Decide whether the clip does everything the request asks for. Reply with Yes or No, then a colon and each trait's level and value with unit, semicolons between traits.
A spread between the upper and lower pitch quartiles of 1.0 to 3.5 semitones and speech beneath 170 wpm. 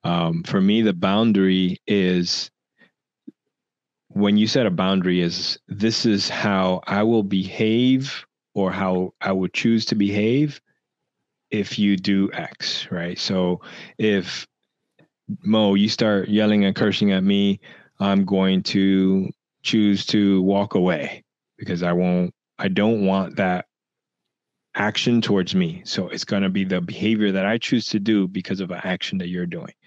Yes: narrow, 2.5 semitones; average, 150 wpm